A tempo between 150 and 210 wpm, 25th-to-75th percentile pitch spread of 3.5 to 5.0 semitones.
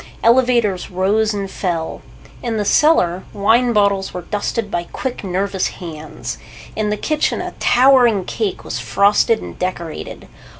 No: average, 140 wpm; average, 4.2 semitones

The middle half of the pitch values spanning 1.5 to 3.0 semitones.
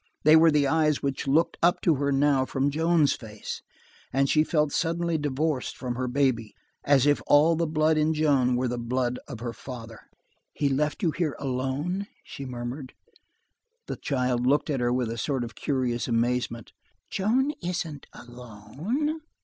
No: average, 3.9 semitones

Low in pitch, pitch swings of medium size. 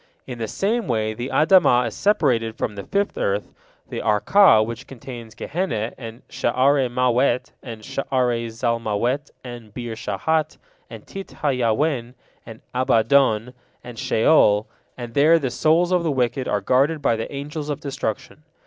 Yes: low, 125 Hz; average, 4.2 semitones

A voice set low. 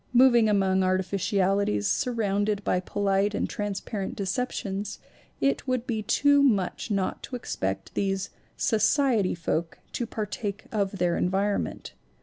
No: high, 200 Hz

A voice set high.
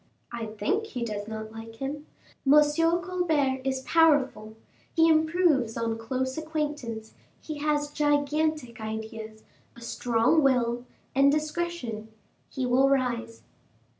Yes: very high, 265 Hz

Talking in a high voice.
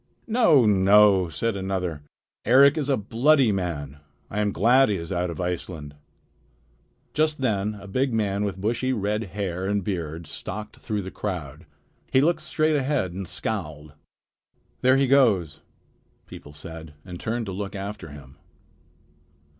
No: low, 100 Hz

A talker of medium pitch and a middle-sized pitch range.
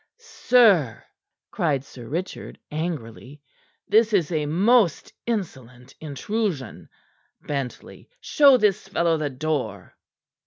No: medium, 155 Hz; wide, 7.4 semitones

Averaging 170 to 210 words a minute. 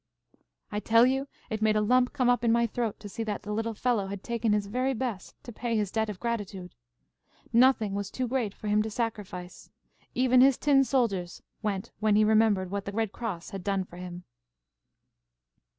Yes: average, 200 wpm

